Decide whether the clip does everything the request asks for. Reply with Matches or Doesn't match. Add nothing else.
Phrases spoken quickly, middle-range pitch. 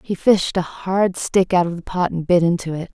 Matches